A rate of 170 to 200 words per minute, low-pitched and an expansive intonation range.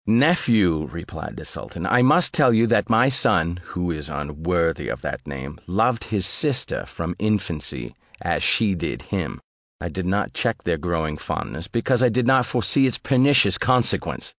Yes: average, 175 wpm; low, 105 Hz; wide, 6.9 semitones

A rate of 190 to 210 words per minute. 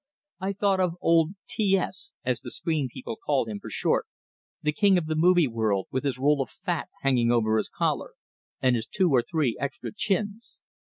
Yes: average, 200 wpm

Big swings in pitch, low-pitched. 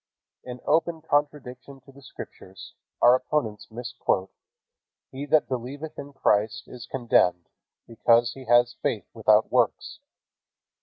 No: average, 3.4 semitones; low, 125 Hz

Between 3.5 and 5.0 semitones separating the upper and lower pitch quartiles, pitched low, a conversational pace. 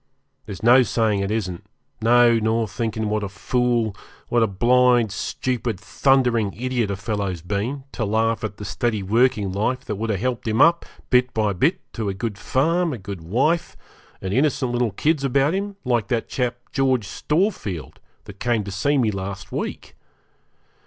Yes: average, 3.8 semitones; low, 115 Hz; average, 175 wpm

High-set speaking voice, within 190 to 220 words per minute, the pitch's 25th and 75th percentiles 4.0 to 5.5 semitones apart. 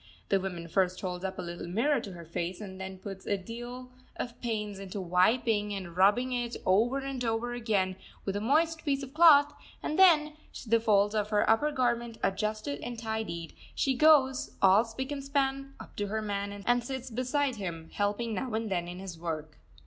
Yes: high, 220 Hz; average, 195 wpm; average, 5.0 semitones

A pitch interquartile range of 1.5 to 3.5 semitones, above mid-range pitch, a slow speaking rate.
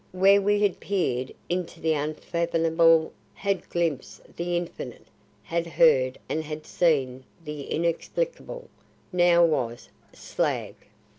No: average, 2.9 semitones; medium, 170 Hz; slow, 115 wpm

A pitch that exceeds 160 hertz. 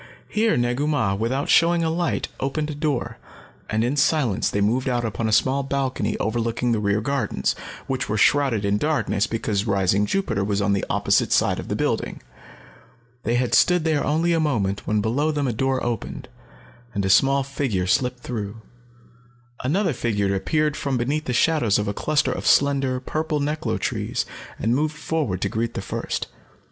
No: low, 130 Hz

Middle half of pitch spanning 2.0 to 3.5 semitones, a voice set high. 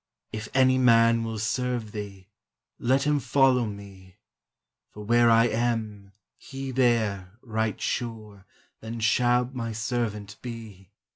No: average, 2.7 semitones; low, 115 Hz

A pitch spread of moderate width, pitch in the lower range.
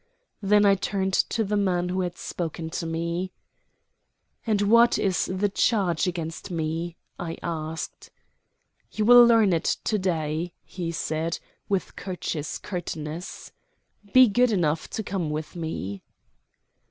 No: average, 3.7 semitones; medium, 180 Hz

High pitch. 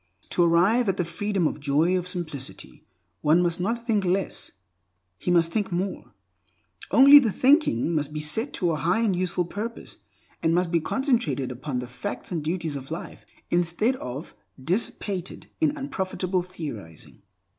No: medium, 180 Hz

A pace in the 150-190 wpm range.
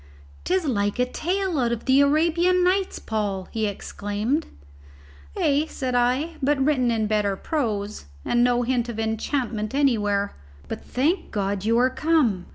Yes: average, 155 wpm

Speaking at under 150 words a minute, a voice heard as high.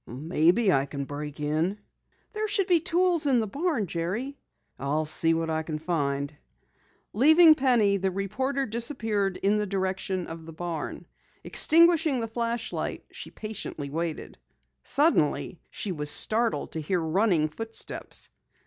Yes: average, 140 wpm; high, 195 Hz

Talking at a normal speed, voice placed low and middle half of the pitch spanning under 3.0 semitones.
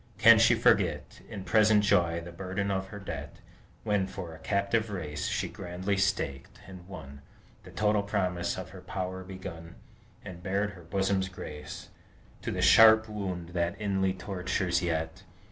Yes: average, 160 wpm; very low, 95 Hz; narrow, 2.5 semitones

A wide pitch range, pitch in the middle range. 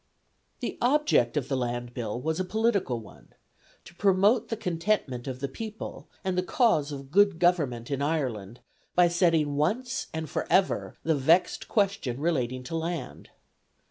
Yes: wide, 7.0 semitones; medium, 160 Hz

